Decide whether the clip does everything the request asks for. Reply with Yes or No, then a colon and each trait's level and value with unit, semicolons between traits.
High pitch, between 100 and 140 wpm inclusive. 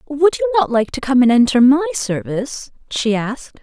No: very high, 260 Hz; average, 200 wpm